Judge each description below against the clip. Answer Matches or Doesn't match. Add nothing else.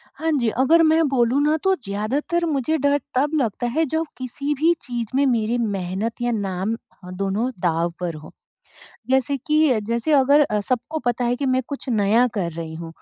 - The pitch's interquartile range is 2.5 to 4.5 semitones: Doesn't match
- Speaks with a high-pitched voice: Matches